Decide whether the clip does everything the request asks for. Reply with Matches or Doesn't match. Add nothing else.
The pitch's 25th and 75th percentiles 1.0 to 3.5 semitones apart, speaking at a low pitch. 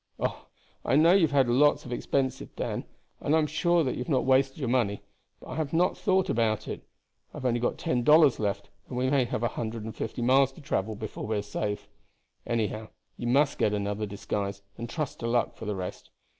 Doesn't match